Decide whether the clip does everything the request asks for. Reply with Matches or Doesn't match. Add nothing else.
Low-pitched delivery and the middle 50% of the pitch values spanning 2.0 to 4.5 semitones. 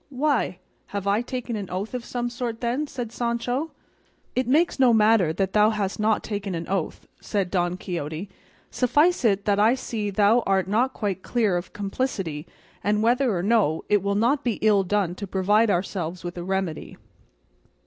Doesn't match